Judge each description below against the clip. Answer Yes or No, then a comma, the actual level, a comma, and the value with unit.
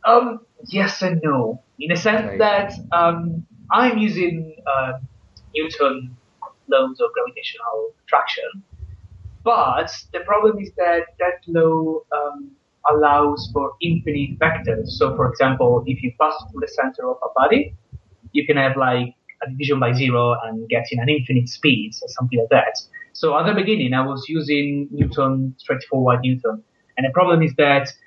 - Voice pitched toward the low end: No, medium, 150 Hz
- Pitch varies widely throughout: Yes, wide, 6.0 semitones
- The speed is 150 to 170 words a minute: Yes, average, 160 wpm